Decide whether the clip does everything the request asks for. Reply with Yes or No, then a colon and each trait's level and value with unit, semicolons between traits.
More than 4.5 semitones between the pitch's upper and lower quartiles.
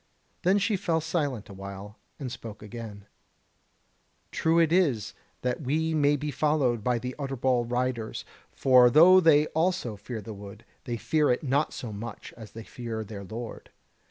Yes: wide, 5.5 semitones